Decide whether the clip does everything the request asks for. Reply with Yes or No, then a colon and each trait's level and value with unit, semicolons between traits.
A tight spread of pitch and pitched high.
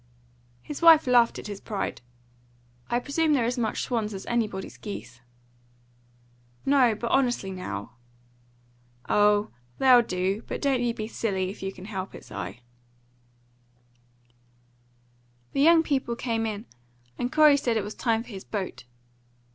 No: average, 4.3 semitones; high, 225 Hz